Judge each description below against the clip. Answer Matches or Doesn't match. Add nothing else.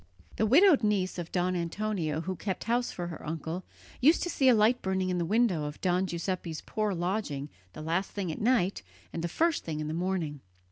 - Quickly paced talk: Matches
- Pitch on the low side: Doesn't match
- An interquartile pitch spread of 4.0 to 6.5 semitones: Matches